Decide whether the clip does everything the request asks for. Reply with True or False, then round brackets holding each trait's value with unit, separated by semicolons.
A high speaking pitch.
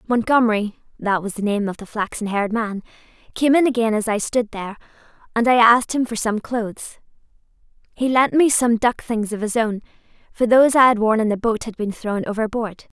True (225 Hz)